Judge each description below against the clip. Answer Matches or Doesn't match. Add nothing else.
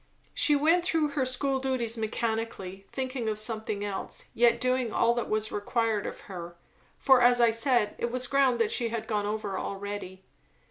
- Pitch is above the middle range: Matches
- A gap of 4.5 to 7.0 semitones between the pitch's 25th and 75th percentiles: Doesn't match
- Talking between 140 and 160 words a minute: Doesn't match